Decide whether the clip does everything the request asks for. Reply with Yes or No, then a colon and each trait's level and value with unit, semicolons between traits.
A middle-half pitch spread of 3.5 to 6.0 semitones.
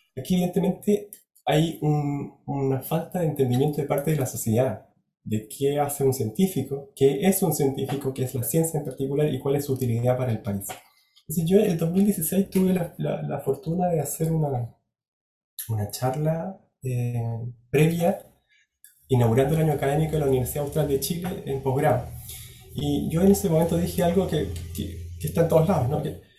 Yes: average, 4.6 semitones